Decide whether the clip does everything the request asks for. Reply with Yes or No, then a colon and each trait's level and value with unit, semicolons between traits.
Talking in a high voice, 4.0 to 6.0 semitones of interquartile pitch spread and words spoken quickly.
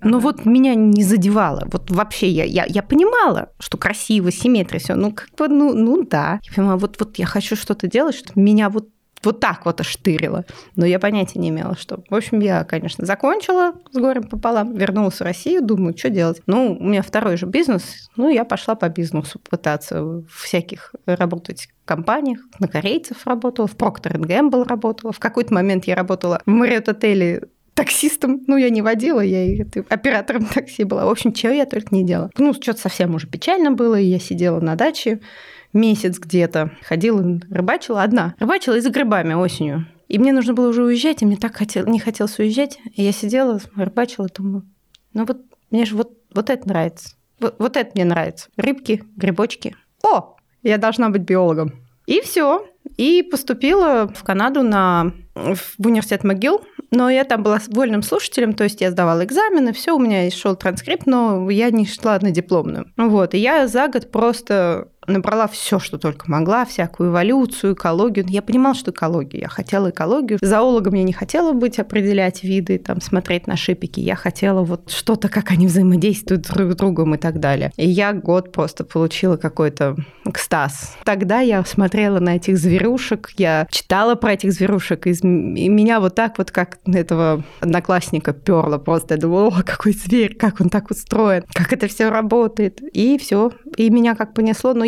Yes: high, 205 Hz; average, 4.6 semitones; fast, 180 wpm